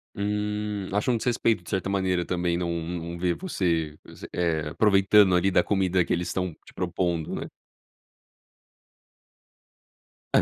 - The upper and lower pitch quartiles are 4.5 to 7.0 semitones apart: No, average, 2.9 semitones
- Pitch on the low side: Yes, very low, 90 Hz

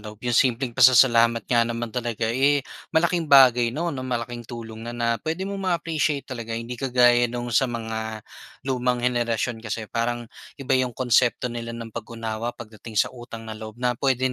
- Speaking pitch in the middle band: No, low, 120 Hz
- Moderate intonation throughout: No, narrow, 2.0 semitones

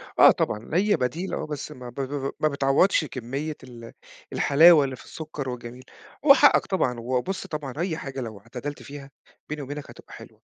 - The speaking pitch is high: No, medium, 140 Hz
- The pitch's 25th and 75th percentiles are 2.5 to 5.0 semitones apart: Yes, average, 3.6 semitones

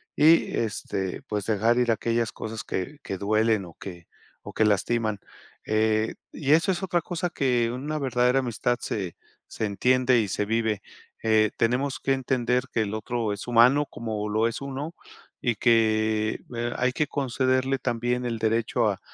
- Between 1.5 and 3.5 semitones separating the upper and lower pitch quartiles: Yes, average, 2.9 semitones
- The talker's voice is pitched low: Yes, low, 115 Hz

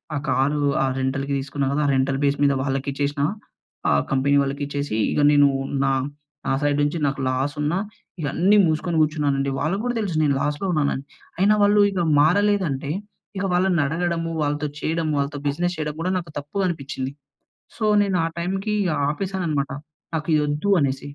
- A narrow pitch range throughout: No, average, 3.7 semitones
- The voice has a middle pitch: Yes, medium, 150 Hz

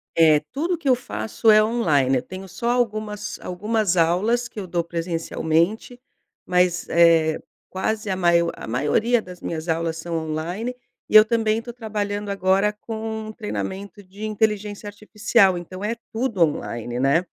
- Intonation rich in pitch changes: No, average, 4.4 semitones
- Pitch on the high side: Yes, high, 200 Hz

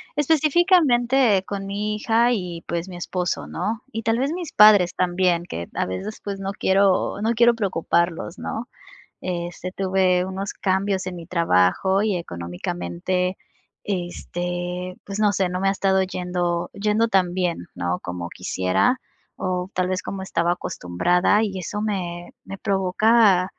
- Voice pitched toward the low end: No, medium, 185 Hz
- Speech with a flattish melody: No, average, 3.0 semitones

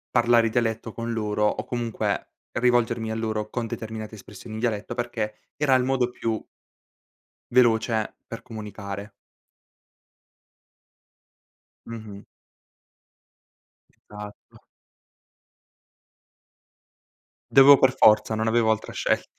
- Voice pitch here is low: Yes, low, 115 Hz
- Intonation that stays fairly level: Yes, narrow, 1.9 semitones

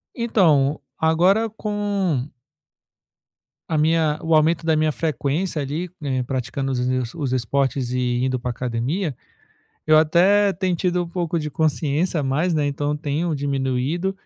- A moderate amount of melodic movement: Yes, average, 4.2 semitones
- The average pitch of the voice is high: No, medium, 155 Hz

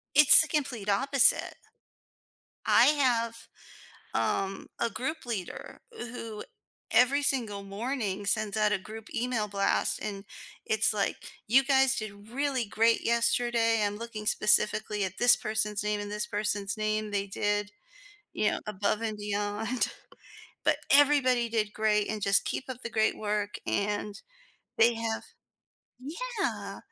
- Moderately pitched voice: No, high, 215 Hz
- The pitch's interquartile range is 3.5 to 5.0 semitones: No, average, 2.9 semitones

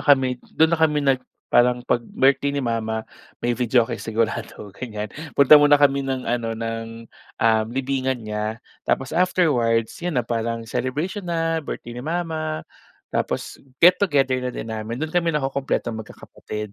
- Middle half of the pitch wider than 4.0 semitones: Yes, average, 4.5 semitones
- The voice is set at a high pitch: No, low, 130 Hz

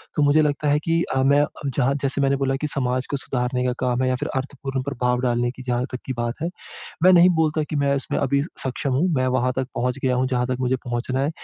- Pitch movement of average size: No, narrow, 2.1 semitones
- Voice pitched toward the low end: Yes, low, 130 Hz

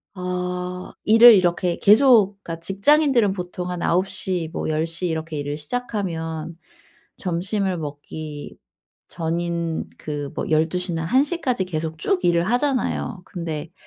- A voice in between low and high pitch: Yes, medium, 180 Hz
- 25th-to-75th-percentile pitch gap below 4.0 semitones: Yes, average, 3.4 semitones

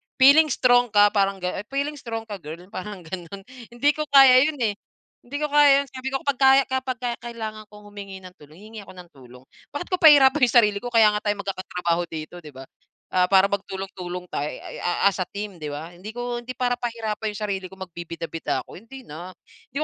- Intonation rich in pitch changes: Yes, wide, 5.7 semitones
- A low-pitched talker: No, high, 210 Hz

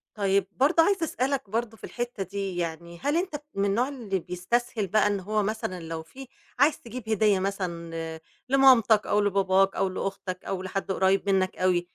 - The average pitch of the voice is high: Yes, high, 200 Hz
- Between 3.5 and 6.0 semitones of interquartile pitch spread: Yes, average, 4.2 semitones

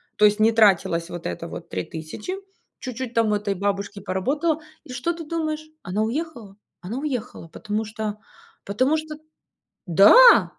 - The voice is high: Yes, high, 220 Hz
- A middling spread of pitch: No, wide, 6.7 semitones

